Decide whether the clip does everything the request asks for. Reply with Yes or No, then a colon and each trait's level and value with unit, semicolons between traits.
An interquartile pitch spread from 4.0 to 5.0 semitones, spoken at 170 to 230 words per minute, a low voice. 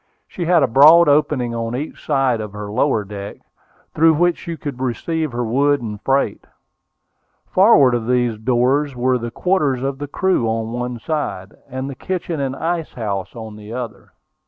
Yes: average, 4.5 semitones; average, 180 wpm; low, 130 Hz